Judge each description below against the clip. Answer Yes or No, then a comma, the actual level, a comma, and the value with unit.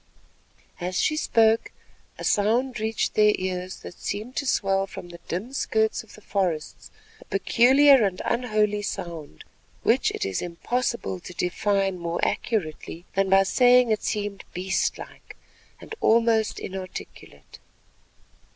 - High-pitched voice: Yes, high, 205 Hz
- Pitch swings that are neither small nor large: Yes, average, 3.9 semitones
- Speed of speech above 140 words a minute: No, slow, 135 wpm